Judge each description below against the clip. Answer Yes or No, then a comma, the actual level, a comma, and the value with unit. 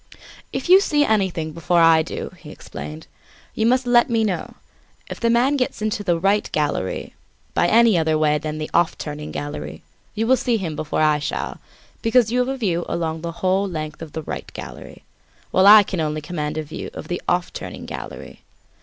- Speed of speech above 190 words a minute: Yes, average, 200 wpm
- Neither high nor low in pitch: Yes, medium, 175 Hz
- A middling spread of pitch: No, wide, 6.4 semitones